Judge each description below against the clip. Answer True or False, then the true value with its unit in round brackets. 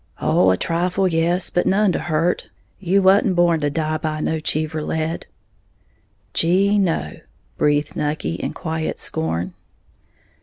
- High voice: False (160 Hz)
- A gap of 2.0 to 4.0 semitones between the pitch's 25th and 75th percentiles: True (2.8 semitones)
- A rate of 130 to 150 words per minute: True (145 wpm)